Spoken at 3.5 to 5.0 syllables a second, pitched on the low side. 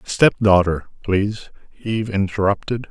Yes: 4.9 syllables/s; low, 100 Hz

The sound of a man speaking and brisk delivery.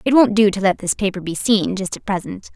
No: female; fast, 280 wpm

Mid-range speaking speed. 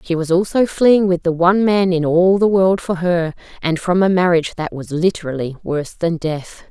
No: fast, 215 wpm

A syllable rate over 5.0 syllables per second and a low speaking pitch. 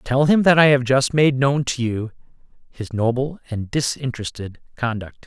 No: 4.8 syllables/s; low, 130 Hz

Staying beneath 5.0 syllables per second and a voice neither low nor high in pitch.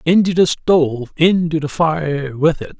Yes: 4.2 syllables/s; medium, 155 Hz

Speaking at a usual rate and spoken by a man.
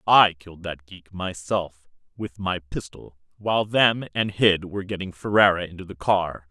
Yes: average, 165 wpm; male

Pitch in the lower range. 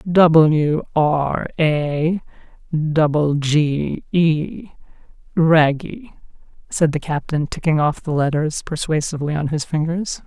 No: medium, 155 Hz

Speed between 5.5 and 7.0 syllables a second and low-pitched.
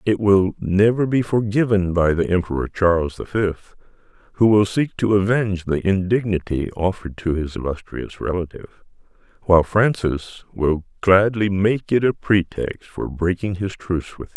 No: 4.9 syllables/s; very low, 95 Hz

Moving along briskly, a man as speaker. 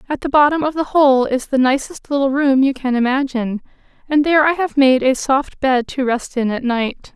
No: fast, 225 wpm; female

